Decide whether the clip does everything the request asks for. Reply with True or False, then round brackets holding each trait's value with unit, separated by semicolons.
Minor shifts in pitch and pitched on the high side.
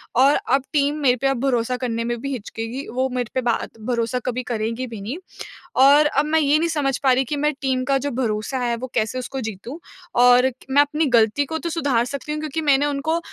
False (3.2 semitones; 265 Hz)